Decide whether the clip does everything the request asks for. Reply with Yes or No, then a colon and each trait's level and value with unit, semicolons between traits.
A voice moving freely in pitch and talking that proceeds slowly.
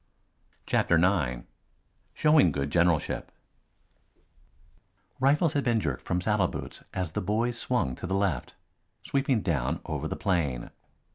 Yes: wide, 7.5 semitones; slow, 130 wpm